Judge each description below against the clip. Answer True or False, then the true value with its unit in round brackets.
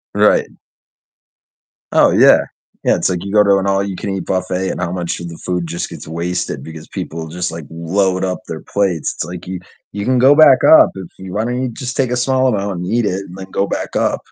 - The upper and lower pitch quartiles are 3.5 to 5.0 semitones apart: False (2.8 semitones)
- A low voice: True (95 Hz)